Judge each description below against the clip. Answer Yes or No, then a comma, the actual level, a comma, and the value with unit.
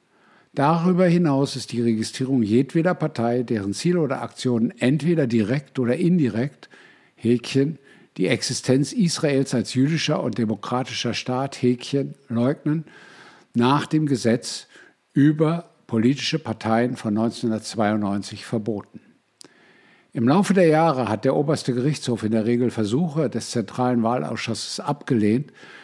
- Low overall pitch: Yes, low, 125 Hz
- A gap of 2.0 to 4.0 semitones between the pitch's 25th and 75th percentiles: No, average, 4.4 semitones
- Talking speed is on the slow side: Yes, slow, 120 wpm